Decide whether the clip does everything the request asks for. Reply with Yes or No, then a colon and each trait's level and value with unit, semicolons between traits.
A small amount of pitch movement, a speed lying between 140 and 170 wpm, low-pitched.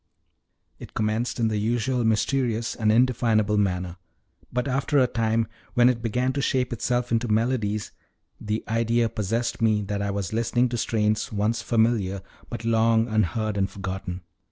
Yes: narrow, 2.2 semitones; average, 155 wpm; low, 115 Hz